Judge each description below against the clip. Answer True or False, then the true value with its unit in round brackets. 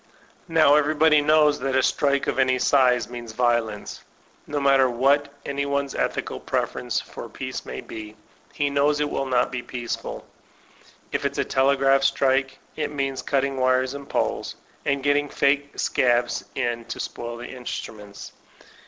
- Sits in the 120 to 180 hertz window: True (135 Hz)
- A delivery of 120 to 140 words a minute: False (155 wpm)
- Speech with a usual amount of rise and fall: False (2.3 semitones)